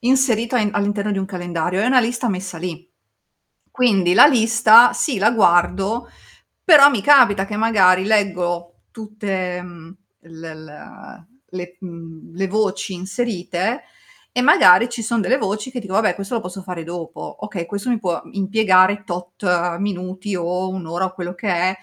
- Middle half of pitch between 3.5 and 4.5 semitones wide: Yes, average, 3.9 semitones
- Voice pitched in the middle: No, high, 195 Hz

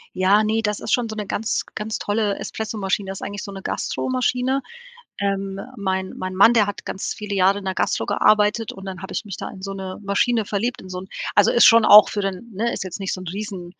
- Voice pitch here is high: Yes, high, 200 Hz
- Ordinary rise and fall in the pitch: No, narrow, 2.2 semitones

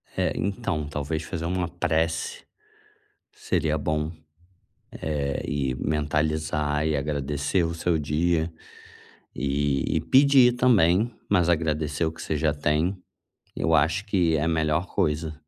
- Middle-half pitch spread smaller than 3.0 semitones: Yes, narrow, 2.4 semitones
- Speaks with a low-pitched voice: Yes, very low, 80 Hz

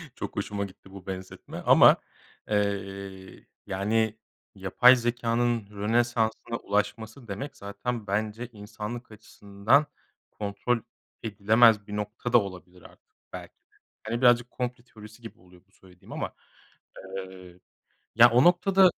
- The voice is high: No, low, 105 Hz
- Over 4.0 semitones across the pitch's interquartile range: No, average, 3.3 semitones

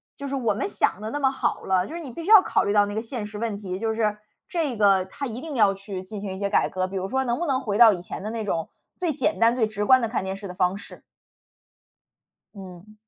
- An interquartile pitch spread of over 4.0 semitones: Yes, average, 4.5 semitones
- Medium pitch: No, high, 215 Hz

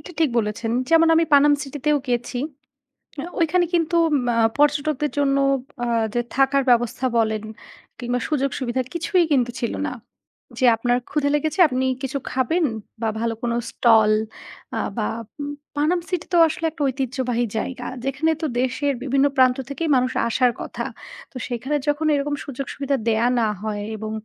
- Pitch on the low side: No, very high, 270 Hz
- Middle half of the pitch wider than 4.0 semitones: No, average, 3.5 semitones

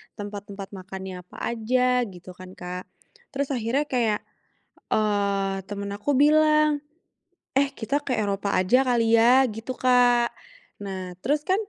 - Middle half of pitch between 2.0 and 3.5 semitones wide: No, average, 4.5 semitones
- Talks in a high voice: Yes, high, 225 Hz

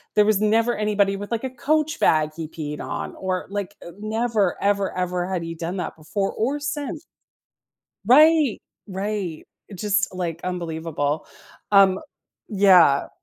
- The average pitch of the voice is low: No, high, 195 Hz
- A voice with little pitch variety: No, average, 3.7 semitones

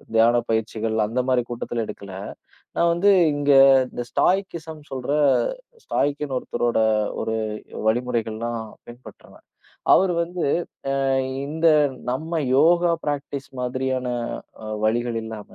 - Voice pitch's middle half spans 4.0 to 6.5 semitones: Yes, average, 4.9 semitones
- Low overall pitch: Yes, low, 130 Hz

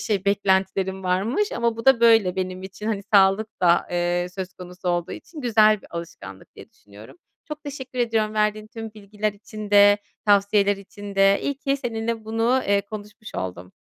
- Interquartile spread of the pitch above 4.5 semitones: No, average, 2.9 semitones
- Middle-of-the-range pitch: No, high, 205 Hz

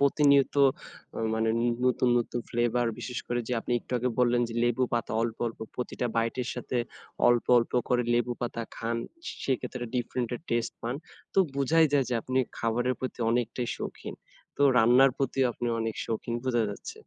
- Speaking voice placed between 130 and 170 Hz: No, low, 120 Hz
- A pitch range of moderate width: No, narrow, 1.5 semitones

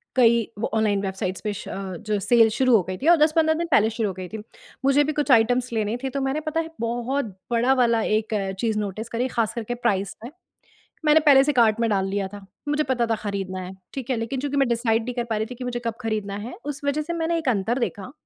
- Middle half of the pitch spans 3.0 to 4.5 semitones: Yes, average, 4.0 semitones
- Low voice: No, high, 235 Hz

